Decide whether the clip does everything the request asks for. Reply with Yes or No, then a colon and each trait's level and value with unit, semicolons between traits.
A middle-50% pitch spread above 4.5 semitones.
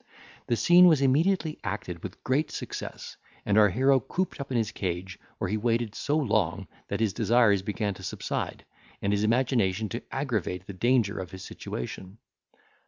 Yes: average, 5.1 semitones